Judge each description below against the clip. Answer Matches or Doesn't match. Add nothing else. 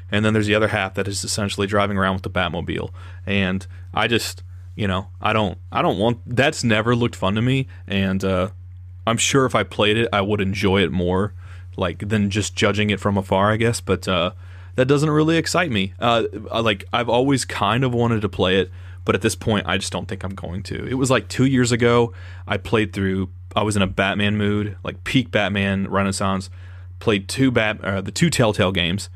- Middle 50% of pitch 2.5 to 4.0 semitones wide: Matches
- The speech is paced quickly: Matches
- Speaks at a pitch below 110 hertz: Matches